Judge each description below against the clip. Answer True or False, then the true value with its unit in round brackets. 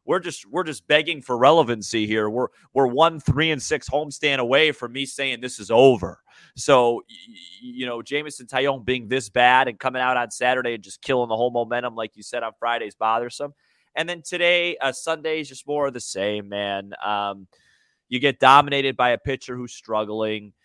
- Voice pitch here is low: True (130 Hz)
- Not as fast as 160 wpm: False (200 wpm)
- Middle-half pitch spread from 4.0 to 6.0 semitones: False (3.6 semitones)